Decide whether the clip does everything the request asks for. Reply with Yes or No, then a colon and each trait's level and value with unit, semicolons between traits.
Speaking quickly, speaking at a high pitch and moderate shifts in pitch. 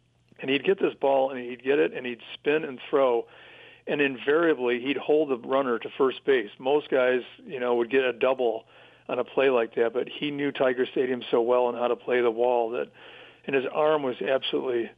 No: fast, 220 wpm; low, 135 Hz; average, 3.7 semitones